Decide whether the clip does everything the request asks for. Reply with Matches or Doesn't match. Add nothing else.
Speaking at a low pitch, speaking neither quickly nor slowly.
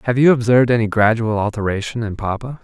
Matches